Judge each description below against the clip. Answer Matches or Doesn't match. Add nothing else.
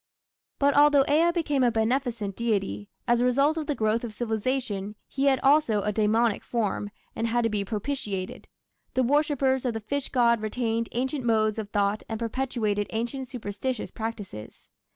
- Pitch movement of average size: Matches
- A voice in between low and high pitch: Doesn't match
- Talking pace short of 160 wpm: Doesn't match